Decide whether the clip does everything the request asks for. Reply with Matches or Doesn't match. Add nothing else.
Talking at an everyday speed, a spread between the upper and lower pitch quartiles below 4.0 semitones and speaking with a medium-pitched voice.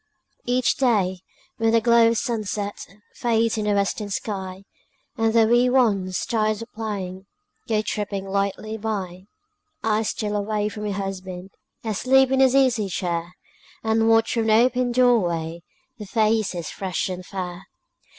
Doesn't match